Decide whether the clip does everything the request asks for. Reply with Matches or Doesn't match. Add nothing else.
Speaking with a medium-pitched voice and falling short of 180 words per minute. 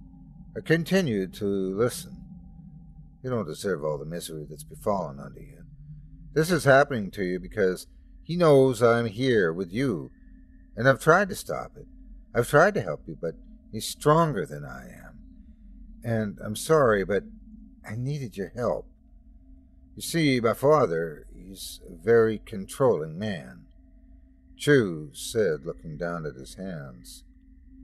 Doesn't match